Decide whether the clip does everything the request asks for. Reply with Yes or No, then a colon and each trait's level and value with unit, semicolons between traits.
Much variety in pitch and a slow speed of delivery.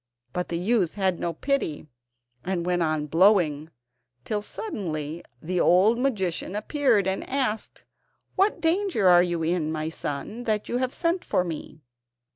No: wide, 6.0 semitones; average, 150 wpm